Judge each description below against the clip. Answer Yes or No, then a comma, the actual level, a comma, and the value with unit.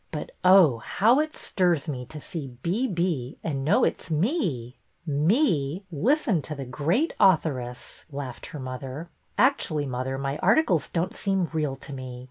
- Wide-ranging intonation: Yes, wide, 5.7 semitones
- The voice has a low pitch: No, medium, 155 Hz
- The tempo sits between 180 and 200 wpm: Yes, average, 185 wpm